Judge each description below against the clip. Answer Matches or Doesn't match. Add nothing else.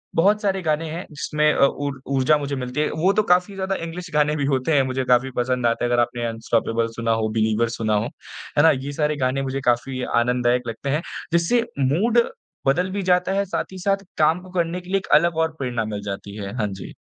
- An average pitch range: Doesn't match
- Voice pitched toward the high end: Doesn't match